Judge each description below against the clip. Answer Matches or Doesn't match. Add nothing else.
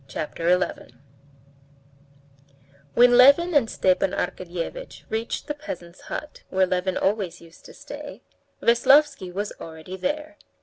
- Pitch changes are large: Matches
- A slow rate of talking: Matches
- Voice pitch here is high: Matches